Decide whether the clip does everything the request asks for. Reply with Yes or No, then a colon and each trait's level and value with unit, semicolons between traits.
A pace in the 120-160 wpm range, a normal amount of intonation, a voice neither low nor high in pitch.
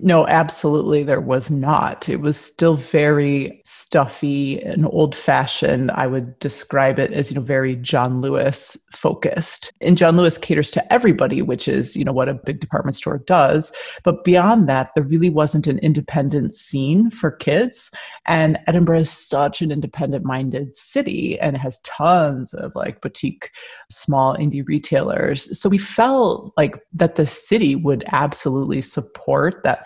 Yes: average, 155 wpm; average, 3.4 semitones; medium, 150 Hz